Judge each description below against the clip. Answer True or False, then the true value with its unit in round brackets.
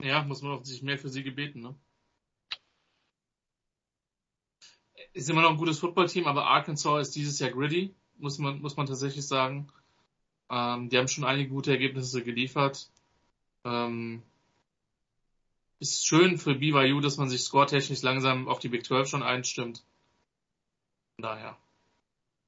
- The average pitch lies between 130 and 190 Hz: True (140 Hz)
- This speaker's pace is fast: False (145 wpm)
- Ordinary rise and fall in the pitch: False (2.3 semitones)